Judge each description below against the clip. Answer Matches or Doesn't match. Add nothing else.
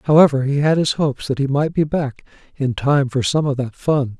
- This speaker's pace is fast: Matches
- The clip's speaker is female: Doesn't match